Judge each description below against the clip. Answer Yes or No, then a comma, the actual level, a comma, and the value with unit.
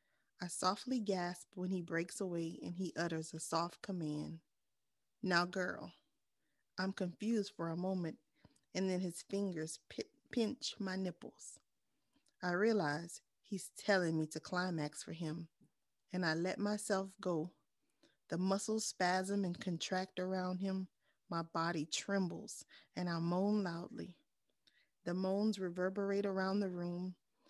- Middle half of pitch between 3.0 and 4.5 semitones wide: No, narrow, 2.6 semitones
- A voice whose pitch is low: No, medium, 185 Hz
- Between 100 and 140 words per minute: Yes, slow, 135 wpm